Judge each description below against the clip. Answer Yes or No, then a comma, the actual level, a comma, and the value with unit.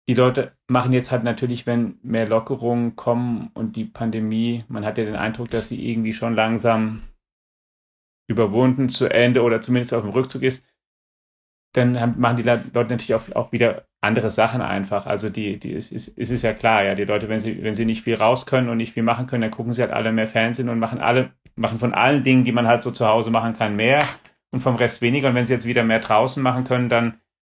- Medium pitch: No, low, 115 Hz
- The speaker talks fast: Yes, fast, 230 wpm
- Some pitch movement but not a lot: No, narrow, 1.9 semitones